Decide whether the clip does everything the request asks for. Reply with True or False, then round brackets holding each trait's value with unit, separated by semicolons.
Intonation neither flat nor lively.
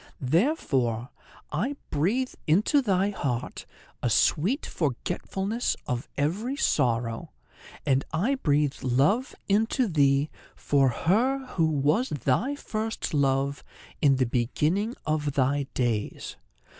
False (8.1 semitones)